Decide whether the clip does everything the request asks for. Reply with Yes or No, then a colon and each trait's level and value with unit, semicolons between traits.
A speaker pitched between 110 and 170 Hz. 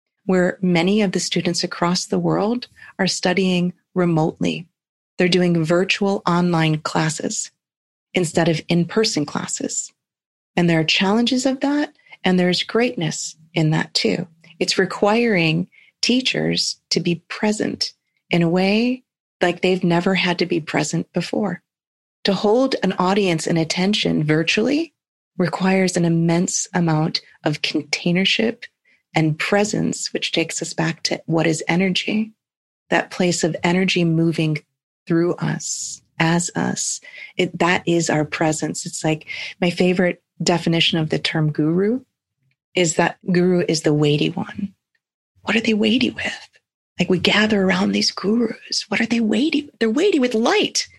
No: medium, 180 Hz